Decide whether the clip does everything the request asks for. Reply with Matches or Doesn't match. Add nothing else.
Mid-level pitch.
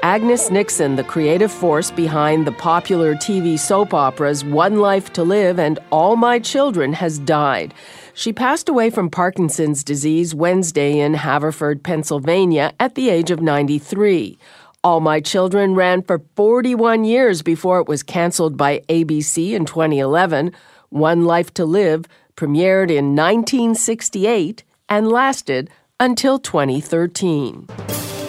Matches